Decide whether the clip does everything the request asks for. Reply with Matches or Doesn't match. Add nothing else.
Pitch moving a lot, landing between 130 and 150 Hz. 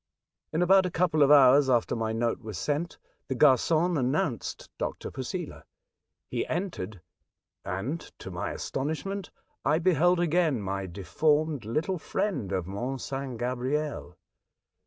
Matches